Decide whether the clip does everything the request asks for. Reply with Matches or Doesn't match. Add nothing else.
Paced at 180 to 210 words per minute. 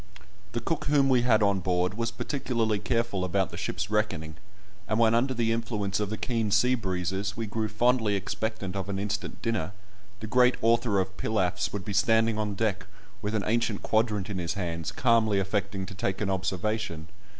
Matches